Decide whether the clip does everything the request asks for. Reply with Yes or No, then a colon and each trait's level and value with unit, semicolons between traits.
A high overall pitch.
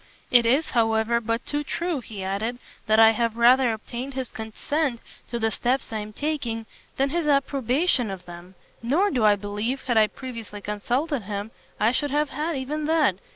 Yes: high, 240 Hz